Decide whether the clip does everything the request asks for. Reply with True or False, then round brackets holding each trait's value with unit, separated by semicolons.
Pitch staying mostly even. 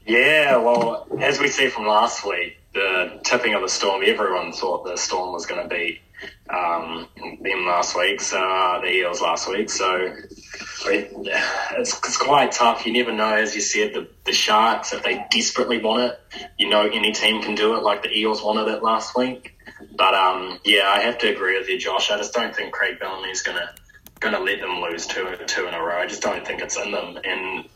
True (2.2 semitones)